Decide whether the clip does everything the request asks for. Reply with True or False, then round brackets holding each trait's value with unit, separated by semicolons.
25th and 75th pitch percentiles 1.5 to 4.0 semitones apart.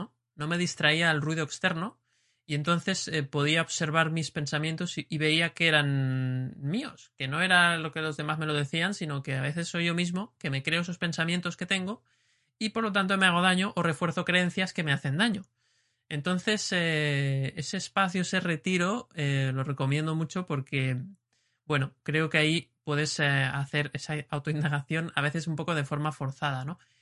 True (3.4 semitones)